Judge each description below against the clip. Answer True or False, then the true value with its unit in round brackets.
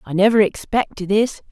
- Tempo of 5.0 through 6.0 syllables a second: True (5.3 syllables/s)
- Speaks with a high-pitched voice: True (205 Hz)